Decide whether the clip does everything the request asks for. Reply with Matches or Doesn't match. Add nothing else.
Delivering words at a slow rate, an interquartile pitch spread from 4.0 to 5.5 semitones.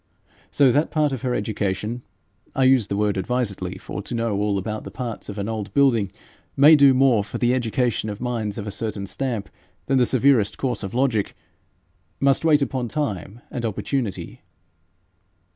Doesn't match